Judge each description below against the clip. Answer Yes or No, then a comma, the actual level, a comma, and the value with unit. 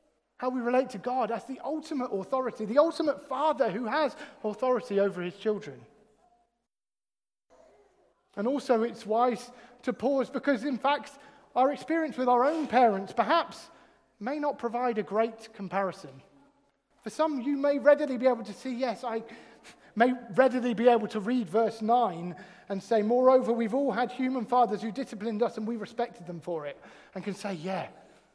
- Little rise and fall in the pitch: No, average, 3.4 semitones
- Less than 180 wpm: Yes, average, 170 wpm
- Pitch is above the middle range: Yes, high, 240 Hz